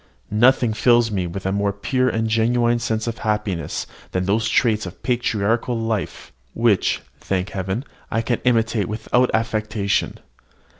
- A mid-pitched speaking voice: No, low, 110 Hz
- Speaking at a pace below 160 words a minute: Yes, average, 145 wpm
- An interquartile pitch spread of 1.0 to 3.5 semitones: Yes, average, 2.8 semitones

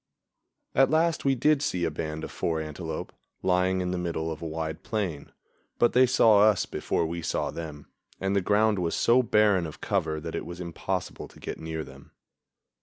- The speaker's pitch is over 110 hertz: No, very low, 90 Hz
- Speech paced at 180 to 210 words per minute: Yes, average, 195 wpm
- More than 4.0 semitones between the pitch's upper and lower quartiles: Yes, average, 5.0 semitones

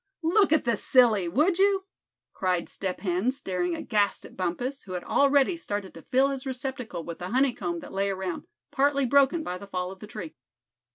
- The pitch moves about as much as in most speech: No, wide, 7.1 semitones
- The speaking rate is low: No, average, 195 wpm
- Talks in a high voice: Yes, high, 220 Hz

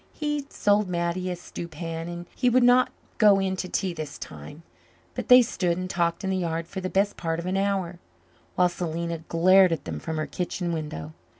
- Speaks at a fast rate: Yes, fast, 210 wpm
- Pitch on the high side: No, medium, 175 Hz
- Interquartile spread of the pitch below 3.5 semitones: Yes, narrow, 2.5 semitones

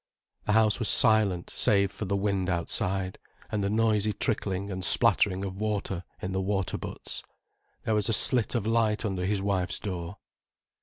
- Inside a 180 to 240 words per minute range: No, average, 170 wpm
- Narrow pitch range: Yes, narrow, 2.3 semitones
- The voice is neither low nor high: No, low, 100 Hz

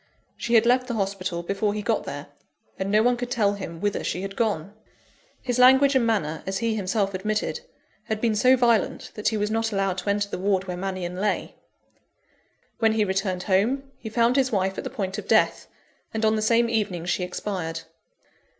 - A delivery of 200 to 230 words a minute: Yes, fast, 205 wpm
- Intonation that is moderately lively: Yes, average, 3.3 semitones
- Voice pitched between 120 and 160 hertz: No, high, 210 Hz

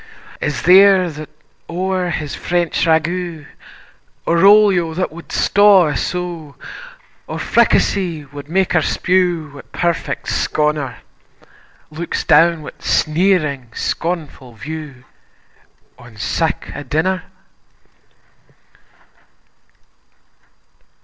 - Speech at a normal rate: No, slow, 95 wpm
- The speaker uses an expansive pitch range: No, average, 3.3 semitones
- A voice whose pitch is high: No, medium, 165 Hz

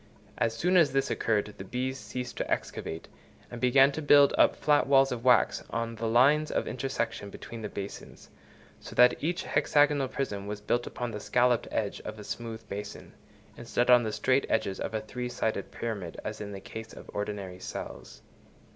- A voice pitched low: Yes, low, 115 Hz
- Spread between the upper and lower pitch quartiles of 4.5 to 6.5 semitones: No, average, 3.8 semitones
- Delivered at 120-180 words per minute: No, average, 190 wpm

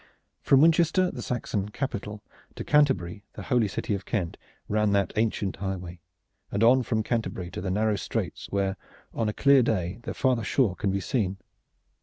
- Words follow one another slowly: No, average, 175 wpm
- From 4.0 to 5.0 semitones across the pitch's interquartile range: Yes, average, 4.3 semitones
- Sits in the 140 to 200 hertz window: No, low, 105 Hz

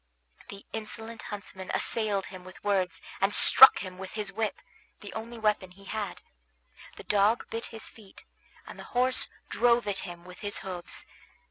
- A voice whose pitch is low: No, high, 205 Hz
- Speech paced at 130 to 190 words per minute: Yes, average, 165 wpm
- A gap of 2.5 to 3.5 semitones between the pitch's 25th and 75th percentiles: Yes, average, 2.8 semitones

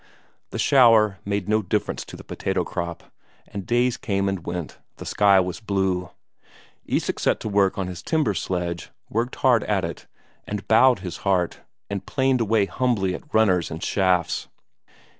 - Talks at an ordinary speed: Yes, average, 165 wpm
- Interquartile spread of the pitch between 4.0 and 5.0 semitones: No, average, 3.4 semitones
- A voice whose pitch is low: Yes, low, 100 Hz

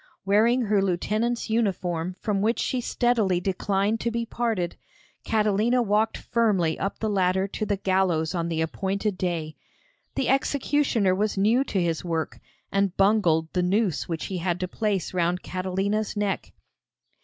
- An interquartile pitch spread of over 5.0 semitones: No, average, 3.4 semitones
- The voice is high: Yes, high, 195 Hz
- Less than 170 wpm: Yes, average, 155 wpm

